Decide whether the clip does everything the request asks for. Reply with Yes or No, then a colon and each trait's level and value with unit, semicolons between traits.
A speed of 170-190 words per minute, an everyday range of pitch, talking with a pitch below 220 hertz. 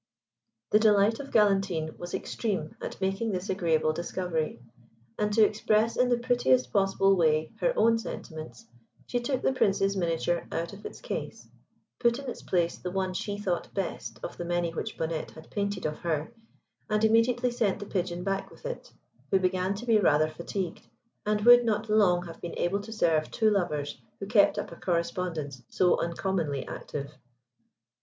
Yes: average, 175 wpm; average, 4.1 semitones; high, 190 Hz